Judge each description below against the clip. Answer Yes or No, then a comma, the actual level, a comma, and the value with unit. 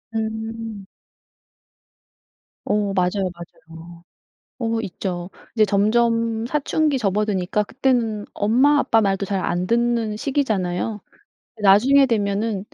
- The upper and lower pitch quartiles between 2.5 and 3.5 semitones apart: Yes, average, 2.8 semitones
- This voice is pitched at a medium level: No, high, 215 Hz